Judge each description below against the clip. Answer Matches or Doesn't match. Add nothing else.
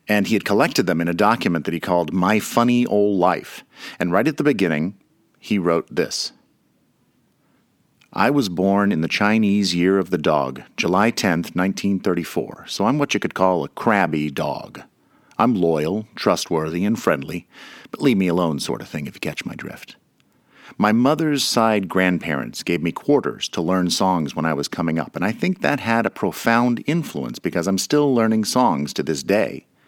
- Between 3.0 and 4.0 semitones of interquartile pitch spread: Doesn't match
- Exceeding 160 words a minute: Matches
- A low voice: Matches